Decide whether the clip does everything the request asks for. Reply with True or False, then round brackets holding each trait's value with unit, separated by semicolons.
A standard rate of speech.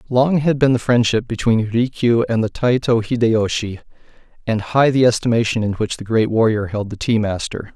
True (185 wpm)